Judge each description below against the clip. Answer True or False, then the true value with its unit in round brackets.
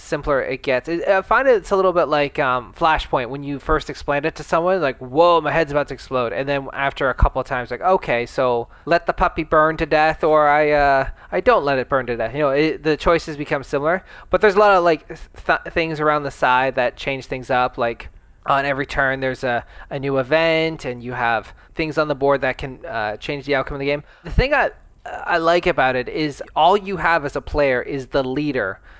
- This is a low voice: False (145 Hz)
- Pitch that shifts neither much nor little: True (3.7 semitones)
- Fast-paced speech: True (240 wpm)